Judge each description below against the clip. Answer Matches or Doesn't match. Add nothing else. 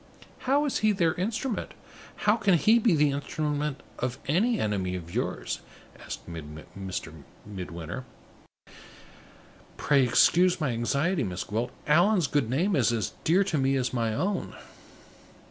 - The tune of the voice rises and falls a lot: Matches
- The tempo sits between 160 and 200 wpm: Doesn't match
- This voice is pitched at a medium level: Matches